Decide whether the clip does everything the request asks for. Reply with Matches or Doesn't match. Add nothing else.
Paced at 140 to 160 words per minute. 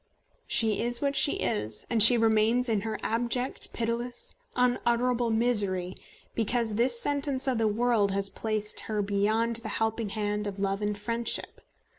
Matches